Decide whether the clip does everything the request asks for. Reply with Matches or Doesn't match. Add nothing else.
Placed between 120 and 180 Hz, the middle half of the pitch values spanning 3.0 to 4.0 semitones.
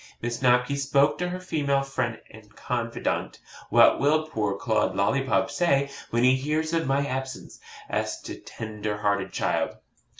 Matches